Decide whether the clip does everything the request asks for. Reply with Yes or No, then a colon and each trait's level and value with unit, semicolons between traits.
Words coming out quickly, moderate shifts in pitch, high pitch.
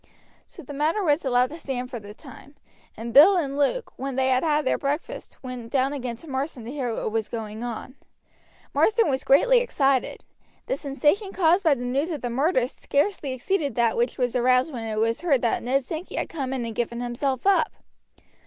Yes: fast, 210 wpm; average, 3.9 semitones; very high, 270 Hz